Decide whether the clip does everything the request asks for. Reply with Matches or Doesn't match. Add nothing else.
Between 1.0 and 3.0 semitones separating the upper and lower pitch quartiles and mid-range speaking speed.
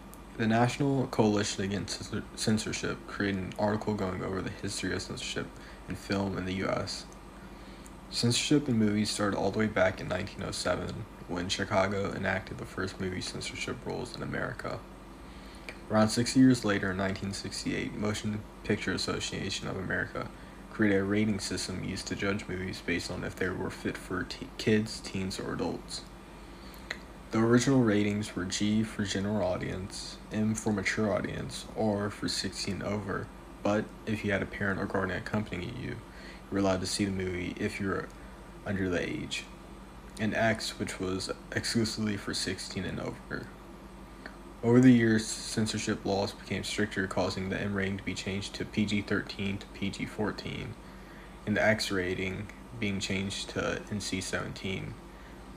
Matches